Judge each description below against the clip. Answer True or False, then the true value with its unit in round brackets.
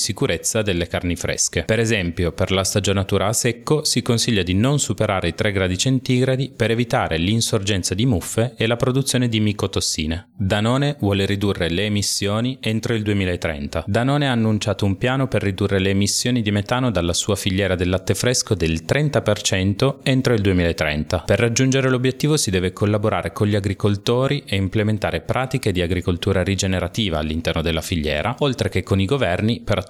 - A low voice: True (105 Hz)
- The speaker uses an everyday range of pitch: True (4.3 semitones)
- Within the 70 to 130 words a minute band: False (170 wpm)